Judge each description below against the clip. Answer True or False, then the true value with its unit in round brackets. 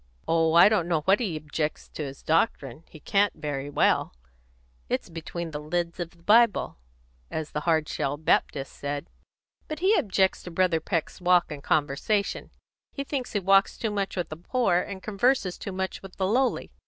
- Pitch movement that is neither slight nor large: True (4.3 semitones)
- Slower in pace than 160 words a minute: False (185 wpm)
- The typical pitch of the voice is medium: True (175 Hz)